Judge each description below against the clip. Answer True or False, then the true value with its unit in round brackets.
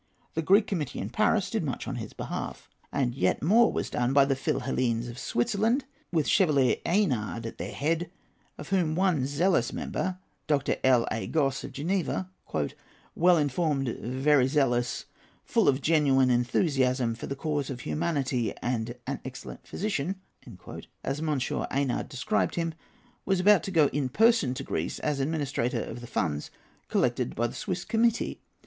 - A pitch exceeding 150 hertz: False (140 Hz)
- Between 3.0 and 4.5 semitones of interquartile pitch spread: False (5.2 semitones)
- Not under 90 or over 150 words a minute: False (160 wpm)